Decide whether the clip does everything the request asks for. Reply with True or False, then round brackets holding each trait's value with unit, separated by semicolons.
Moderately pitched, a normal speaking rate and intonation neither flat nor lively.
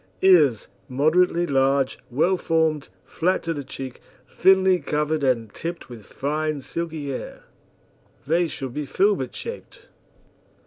False (155 Hz; 125 wpm; 4.2 semitones)